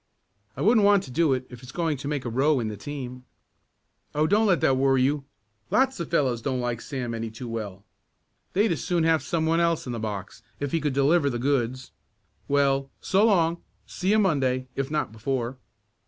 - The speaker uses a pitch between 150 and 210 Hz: No, medium, 140 Hz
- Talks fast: Yes, fast, 215 wpm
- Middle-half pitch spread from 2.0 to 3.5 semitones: No, average, 4.8 semitones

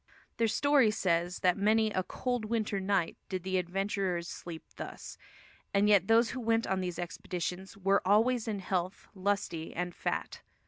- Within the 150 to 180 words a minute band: Yes, average, 165 wpm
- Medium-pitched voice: No, high, 195 Hz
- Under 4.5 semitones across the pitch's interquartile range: Yes, average, 3.3 semitones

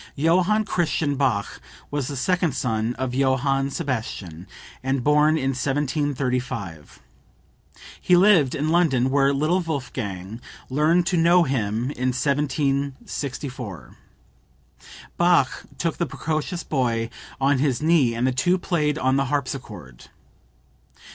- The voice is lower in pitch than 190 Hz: Yes, medium, 140 Hz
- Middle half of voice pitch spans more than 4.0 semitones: No, average, 3.7 semitones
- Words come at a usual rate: No, slow, 120 wpm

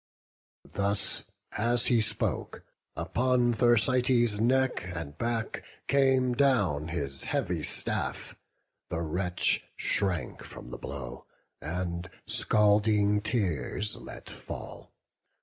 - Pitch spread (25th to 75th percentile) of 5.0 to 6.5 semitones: Yes, wide, 5.6 semitones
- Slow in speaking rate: Yes, slow, 95 wpm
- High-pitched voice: No, low, 105 Hz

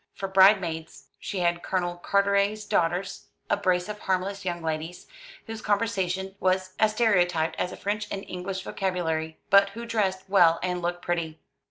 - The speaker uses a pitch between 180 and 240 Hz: Yes, high, 190 Hz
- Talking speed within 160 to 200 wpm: Yes, average, 165 wpm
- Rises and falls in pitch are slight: Yes, narrow, 2.3 semitones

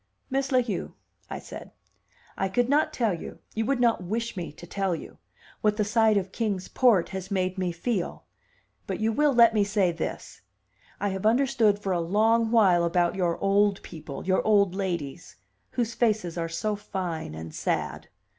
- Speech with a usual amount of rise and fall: Yes, average, 4.0 semitones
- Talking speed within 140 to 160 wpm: No, average, 185 wpm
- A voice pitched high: Yes, high, 200 Hz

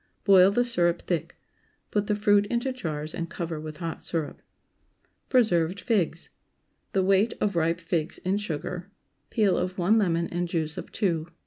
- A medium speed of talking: Yes, average, 165 wpm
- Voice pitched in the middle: Yes, medium, 180 Hz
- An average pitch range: Yes, average, 3.6 semitones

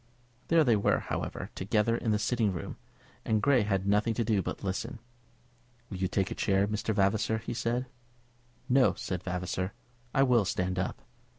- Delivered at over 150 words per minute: Yes, average, 180 wpm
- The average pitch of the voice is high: No, low, 105 Hz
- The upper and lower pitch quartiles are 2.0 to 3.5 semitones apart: Yes, average, 3.2 semitones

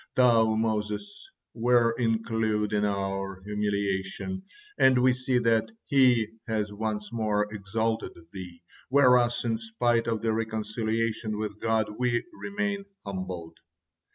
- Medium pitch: No, low, 110 Hz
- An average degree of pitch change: No, narrow, 2.3 semitones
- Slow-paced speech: Yes, slow, 120 wpm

